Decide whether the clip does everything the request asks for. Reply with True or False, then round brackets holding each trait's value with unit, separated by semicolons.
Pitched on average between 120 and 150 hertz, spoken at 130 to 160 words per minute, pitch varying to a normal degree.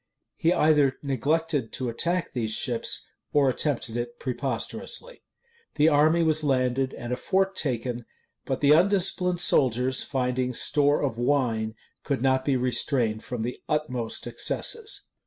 True (135 Hz; 140 wpm; 3.9 semitones)